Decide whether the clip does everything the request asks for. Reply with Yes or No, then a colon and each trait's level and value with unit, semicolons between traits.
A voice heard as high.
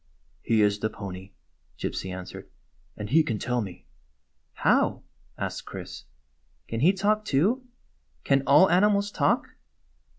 No: low, 135 Hz